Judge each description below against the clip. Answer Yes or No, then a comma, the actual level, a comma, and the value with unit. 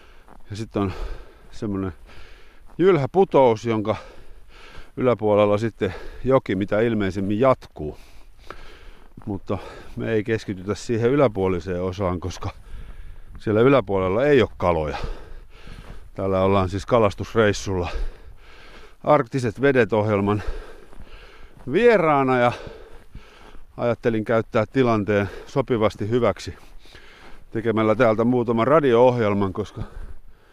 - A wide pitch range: No, average, 3.9 semitones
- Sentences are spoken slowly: Yes, slow, 85 wpm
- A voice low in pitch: Yes, low, 110 Hz